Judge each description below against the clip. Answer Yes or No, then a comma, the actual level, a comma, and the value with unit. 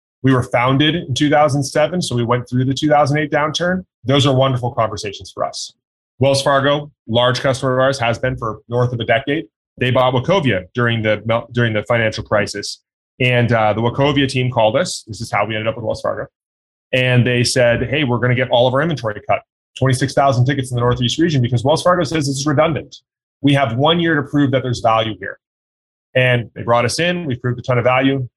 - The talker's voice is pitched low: Yes, low, 125 Hz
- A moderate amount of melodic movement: Yes, average, 3.1 semitones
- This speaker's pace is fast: Yes, fast, 220 wpm